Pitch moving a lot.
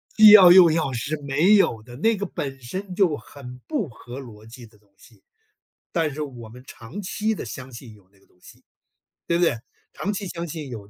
Yes: wide, 7.3 semitones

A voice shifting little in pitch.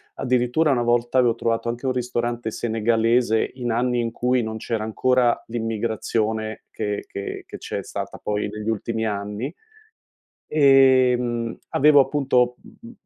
Yes: narrow, 2.1 semitones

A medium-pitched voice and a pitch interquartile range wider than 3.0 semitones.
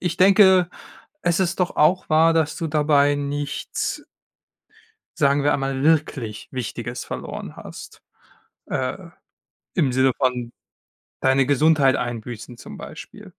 Yes: medium, 145 Hz; average, 3.7 semitones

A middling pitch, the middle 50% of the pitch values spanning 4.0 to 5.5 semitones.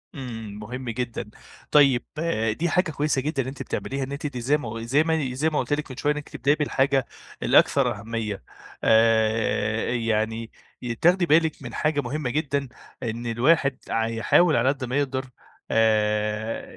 No: low, 130 Hz; average, 4.4 semitones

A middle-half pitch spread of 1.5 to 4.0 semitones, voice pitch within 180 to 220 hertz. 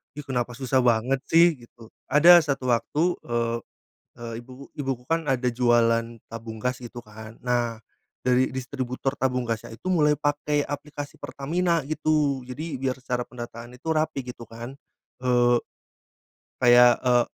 No: average, 3.4 semitones; low, 125 Hz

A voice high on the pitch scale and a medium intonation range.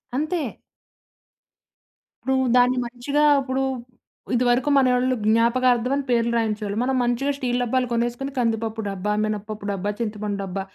Yes: high, 240 Hz; average, 3.0 semitones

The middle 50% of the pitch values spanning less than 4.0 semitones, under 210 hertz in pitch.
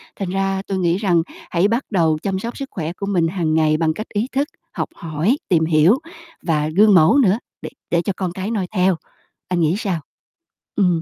Yes: average, 3.6 semitones; medium, 185 Hz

